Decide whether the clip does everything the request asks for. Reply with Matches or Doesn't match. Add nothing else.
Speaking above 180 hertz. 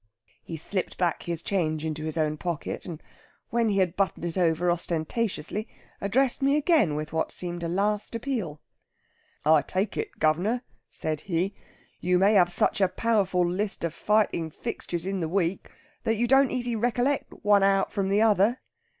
Matches